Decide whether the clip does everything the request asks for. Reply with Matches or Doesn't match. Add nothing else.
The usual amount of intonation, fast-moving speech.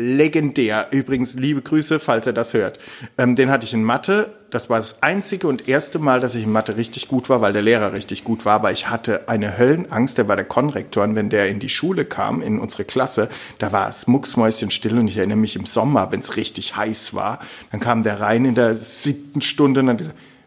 Matches